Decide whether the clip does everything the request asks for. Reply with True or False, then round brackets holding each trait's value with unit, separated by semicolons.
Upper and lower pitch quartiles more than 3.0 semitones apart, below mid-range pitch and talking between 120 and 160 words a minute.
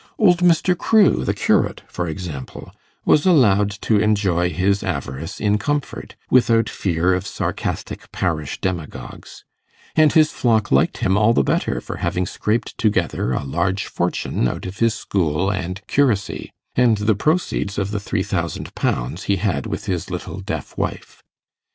True (4.4 semitones; 100 Hz; 155 wpm)